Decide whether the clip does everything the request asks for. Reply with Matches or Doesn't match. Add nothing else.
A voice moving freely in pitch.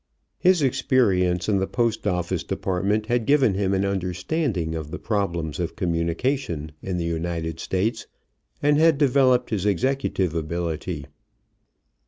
Matches